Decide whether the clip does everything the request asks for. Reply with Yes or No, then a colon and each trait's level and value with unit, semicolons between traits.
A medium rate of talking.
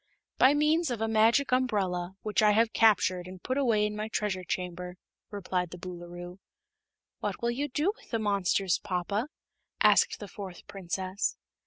Yes: average, 165 wpm